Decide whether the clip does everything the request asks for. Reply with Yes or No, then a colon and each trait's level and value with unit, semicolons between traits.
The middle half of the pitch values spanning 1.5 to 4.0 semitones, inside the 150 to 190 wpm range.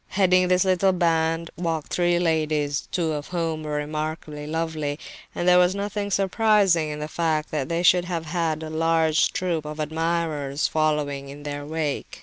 Yes: narrow, 2.5 semitones; average, 170 wpm